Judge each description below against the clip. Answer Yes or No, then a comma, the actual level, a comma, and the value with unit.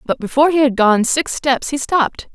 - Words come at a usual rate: No, fast, 230 wpm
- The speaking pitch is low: No, very high, 270 Hz